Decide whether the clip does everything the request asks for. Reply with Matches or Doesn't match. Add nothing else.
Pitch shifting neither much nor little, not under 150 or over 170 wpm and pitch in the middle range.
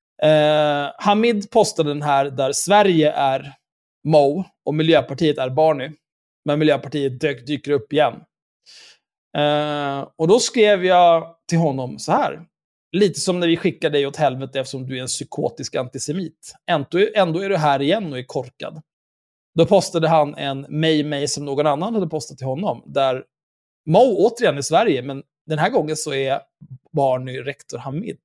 Matches